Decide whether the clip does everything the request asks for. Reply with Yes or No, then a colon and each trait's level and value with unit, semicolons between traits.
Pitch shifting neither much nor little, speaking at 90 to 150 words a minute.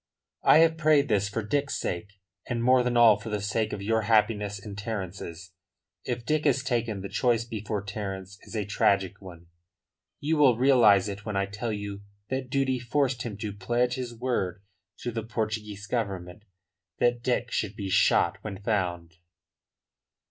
No: average, 3.6 semitones; average, 170 wpm